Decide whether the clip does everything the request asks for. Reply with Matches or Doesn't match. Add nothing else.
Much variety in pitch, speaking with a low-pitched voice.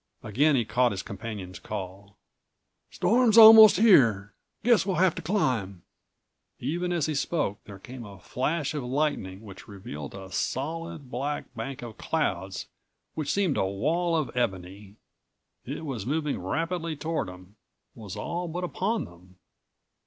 Matches